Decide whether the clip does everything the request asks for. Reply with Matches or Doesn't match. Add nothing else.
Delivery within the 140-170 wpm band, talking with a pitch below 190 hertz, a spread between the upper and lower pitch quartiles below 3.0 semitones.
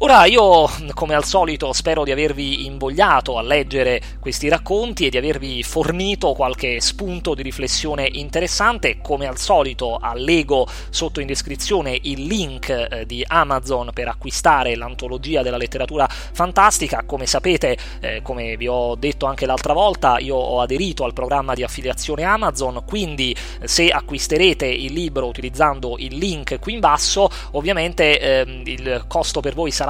Doesn't match